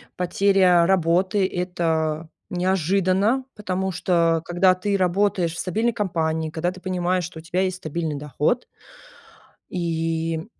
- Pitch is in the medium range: Yes, medium, 180 Hz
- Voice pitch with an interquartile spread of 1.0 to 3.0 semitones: Yes, narrow, 2.5 semitones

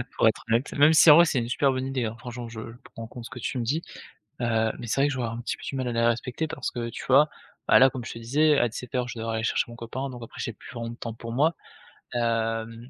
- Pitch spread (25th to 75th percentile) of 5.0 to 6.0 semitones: No, narrow, 2.5 semitones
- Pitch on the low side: Yes, low, 120 Hz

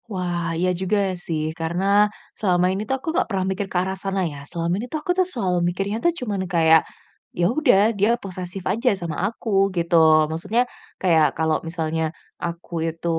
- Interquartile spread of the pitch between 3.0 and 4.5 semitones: Yes, average, 3.4 semitones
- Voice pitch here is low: No, medium, 185 Hz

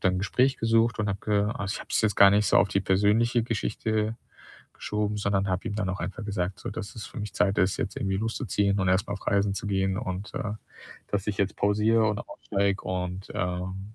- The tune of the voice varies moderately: No, narrow, 1.7 semitones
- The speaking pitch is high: No, low, 100 Hz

